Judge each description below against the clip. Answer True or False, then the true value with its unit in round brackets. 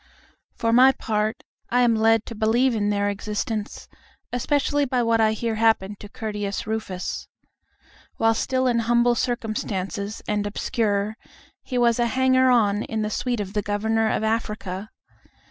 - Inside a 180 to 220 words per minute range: False (155 wpm)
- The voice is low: False (220 Hz)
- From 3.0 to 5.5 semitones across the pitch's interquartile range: False (2.4 semitones)